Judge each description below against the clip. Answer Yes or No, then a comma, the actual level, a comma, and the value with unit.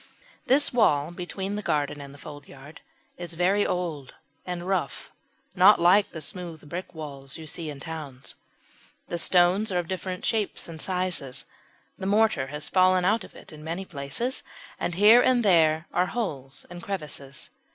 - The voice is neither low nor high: Yes, medium, 175 Hz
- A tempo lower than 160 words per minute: No, average, 165 wpm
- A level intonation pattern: No, average, 4.3 semitones